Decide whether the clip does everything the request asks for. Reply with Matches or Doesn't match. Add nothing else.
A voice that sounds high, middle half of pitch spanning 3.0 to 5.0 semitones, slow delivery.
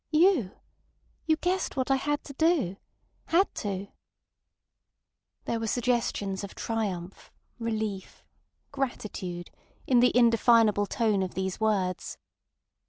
Doesn't match